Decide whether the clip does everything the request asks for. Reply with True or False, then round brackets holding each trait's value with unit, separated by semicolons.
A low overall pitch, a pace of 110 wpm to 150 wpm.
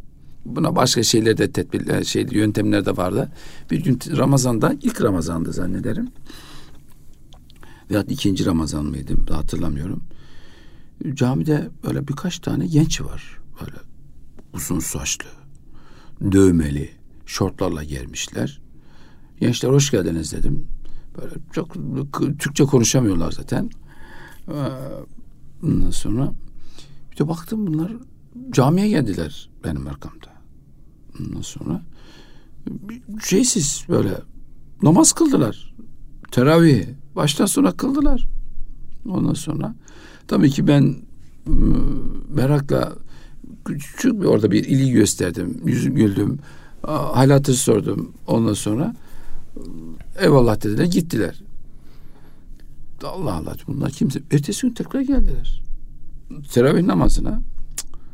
False (130 Hz; 95 wpm)